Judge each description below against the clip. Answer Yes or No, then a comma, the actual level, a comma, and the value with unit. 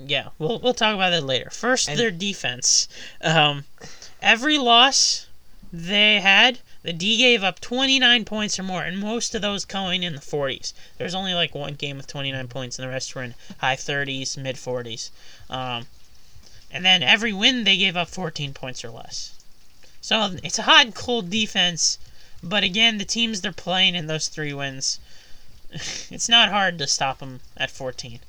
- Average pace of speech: Yes, average, 185 wpm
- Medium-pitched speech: Yes, medium, 175 Hz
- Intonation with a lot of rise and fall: Yes, wide, 8.0 semitones